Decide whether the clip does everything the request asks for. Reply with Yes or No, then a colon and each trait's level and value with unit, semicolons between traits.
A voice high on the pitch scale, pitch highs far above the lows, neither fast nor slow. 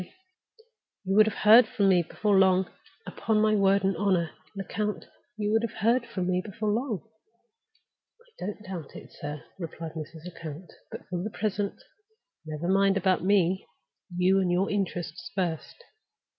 No: high, 195 Hz; average, 2.8 semitones; average, 155 wpm